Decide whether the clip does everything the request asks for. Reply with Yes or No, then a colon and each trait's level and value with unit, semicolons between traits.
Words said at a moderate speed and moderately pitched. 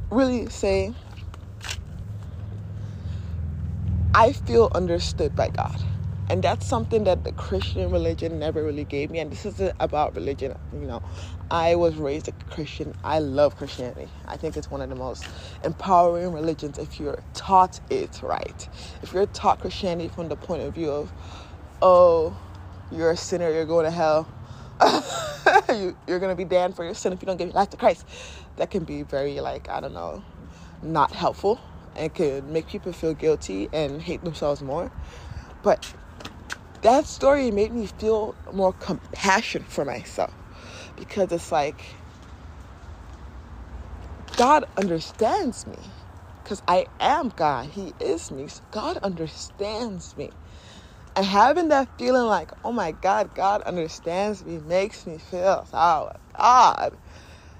Yes: average, 150 wpm; medium, 145 Hz